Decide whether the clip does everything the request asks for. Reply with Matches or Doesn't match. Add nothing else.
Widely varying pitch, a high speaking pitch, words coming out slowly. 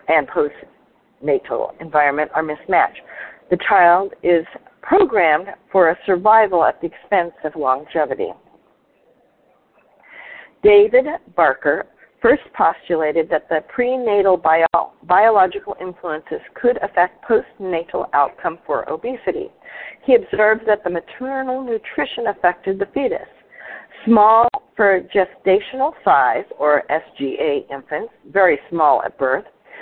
Matches